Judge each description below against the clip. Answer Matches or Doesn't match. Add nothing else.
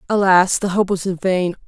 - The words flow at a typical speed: Matches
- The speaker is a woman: Matches